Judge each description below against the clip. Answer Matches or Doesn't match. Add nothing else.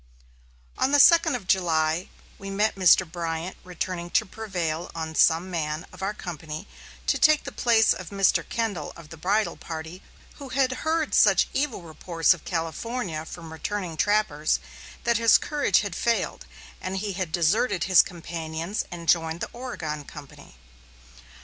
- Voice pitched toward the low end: Doesn't match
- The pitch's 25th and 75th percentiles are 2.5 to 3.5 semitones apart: Doesn't match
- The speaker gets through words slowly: Doesn't match